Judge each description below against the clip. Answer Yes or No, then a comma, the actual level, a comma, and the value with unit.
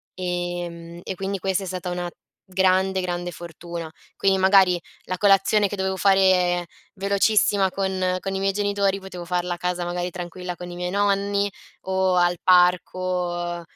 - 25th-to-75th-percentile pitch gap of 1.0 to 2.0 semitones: Yes, narrow, 1.5 semitones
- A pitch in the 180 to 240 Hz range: Yes, medium, 185 Hz